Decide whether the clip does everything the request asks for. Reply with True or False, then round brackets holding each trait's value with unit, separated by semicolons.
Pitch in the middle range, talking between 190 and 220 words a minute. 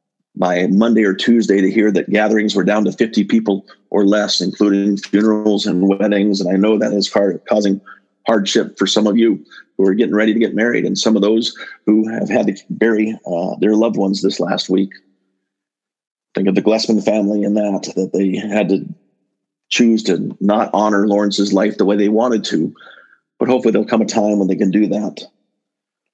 False (105 Hz; 200 wpm)